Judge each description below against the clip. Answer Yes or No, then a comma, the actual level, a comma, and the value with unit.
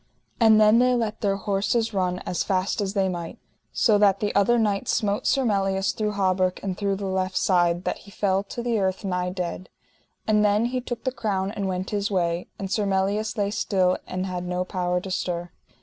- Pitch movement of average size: No, narrow, 2.3 semitones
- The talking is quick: Yes, fast, 210 wpm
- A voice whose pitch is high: Yes, high, 195 Hz